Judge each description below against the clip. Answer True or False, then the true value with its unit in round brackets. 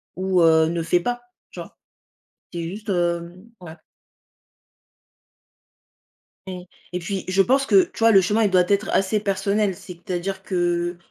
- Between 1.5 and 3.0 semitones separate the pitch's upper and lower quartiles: True (2.5 semitones)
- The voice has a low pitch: False (185 Hz)